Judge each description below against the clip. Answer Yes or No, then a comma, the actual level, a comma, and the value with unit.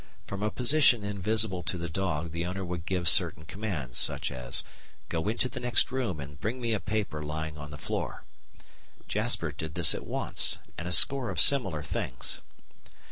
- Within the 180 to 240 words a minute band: Yes, average, 185 wpm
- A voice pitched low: Yes, very low, 90 Hz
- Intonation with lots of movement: Yes, wide, 5.8 semitones